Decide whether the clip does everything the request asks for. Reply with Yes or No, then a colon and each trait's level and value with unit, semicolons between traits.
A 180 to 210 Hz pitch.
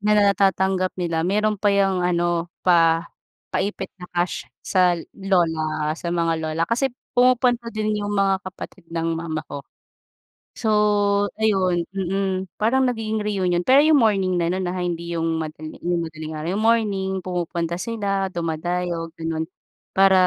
Yes: medium, 185 Hz